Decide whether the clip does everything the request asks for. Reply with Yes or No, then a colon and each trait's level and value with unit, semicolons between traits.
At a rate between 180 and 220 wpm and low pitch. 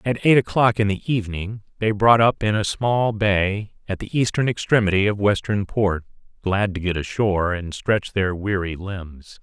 Yes: average, 185 wpm; low, 100 Hz